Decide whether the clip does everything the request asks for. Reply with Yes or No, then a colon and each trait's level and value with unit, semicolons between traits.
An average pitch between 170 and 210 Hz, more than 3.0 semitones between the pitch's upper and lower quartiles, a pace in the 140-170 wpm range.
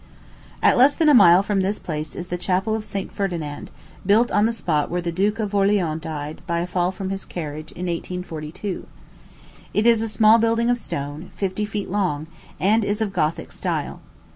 No: high, 190 Hz; average, 3.9 semitones; average, 195 wpm